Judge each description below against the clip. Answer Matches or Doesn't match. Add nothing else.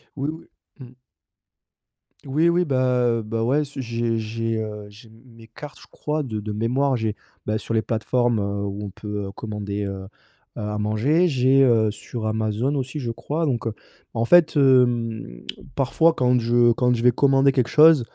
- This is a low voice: Matches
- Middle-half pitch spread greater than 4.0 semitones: Doesn't match